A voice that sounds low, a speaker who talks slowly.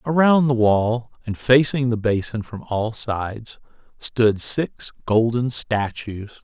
Yes: low, 115 Hz; slow, 130 wpm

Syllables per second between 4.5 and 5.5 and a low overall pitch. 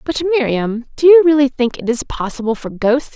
No: 5.4 syllables/s; very high, 265 Hz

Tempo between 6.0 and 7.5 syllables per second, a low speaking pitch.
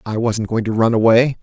No: 5.5 syllables/s; low, 115 Hz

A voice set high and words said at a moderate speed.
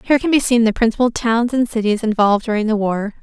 No: high, 225 Hz; fast, 240 wpm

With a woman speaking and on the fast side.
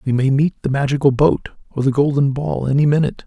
No: male; fast, 220 wpm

